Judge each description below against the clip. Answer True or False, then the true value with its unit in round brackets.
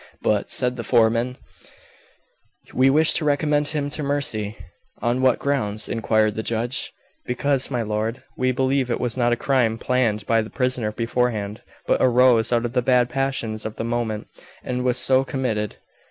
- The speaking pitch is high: False (125 Hz)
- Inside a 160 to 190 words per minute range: True (170 wpm)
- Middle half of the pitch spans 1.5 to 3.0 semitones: True (2.7 semitones)